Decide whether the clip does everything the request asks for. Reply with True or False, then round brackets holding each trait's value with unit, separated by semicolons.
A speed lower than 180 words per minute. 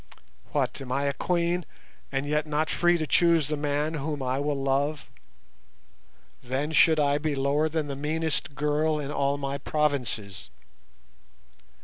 True (150 wpm)